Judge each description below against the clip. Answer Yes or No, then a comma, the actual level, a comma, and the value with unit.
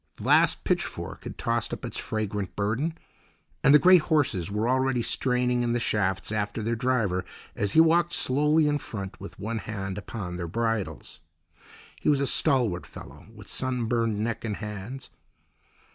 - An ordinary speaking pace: Yes, average, 165 wpm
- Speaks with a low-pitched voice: Yes, low, 115 Hz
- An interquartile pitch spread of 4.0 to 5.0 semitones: Yes, average, 4.3 semitones